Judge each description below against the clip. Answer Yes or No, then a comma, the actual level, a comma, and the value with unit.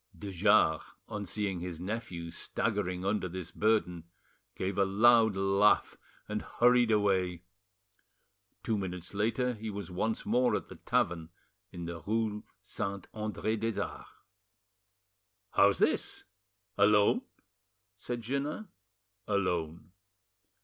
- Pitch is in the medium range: No, low, 100 Hz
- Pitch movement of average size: Yes, average, 3.4 semitones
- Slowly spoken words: Yes, slow, 115 wpm